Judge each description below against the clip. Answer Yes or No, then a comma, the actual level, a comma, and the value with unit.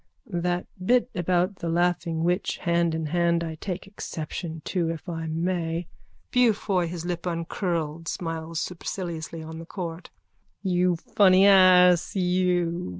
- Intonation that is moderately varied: No, narrow, 1.7 semitones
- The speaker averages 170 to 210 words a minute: No, average, 140 wpm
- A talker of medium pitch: Yes, medium, 175 Hz